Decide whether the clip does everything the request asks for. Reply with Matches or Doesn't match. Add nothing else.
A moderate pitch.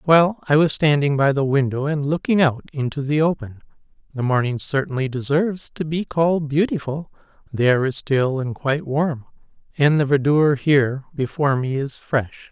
Matches